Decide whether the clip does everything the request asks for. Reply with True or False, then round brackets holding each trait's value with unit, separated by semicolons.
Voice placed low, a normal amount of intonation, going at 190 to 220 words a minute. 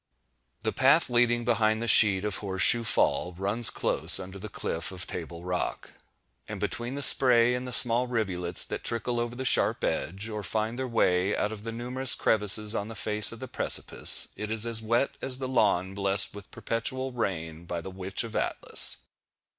True (110 Hz; 3.6 semitones; 195 wpm)